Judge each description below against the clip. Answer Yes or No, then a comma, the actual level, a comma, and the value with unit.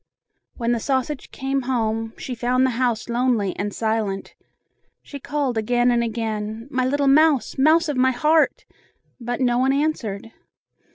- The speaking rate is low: No, average, 155 wpm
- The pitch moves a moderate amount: Yes, average, 3.1 semitones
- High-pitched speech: Yes, high, 245 Hz